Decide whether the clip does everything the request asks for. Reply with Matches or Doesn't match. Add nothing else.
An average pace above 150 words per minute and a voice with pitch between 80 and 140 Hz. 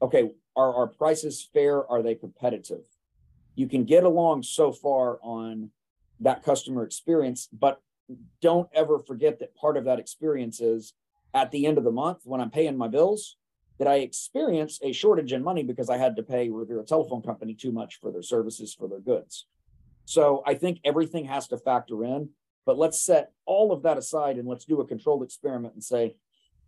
Matches